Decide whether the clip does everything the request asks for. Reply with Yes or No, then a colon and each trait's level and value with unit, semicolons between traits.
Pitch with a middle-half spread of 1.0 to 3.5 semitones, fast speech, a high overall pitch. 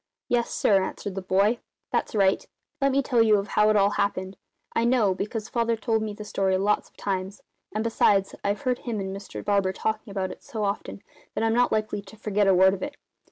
Yes: narrow, 2.5 semitones; fast, 220 wpm; high, 210 Hz